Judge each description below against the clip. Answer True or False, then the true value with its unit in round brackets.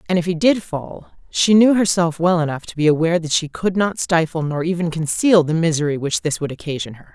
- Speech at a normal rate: False (235 wpm)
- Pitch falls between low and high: True (165 Hz)